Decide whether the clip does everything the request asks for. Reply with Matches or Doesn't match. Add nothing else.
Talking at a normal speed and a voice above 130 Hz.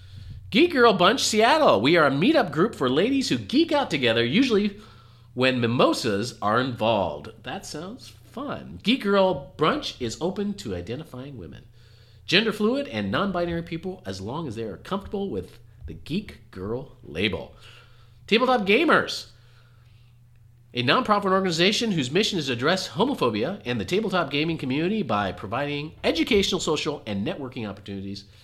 Matches